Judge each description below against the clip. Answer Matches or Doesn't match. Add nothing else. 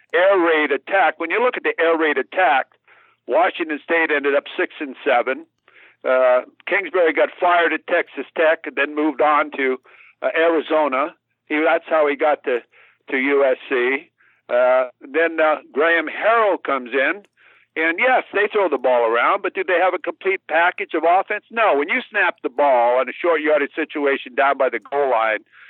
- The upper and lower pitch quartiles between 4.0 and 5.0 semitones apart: Matches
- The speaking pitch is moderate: Matches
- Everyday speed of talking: Matches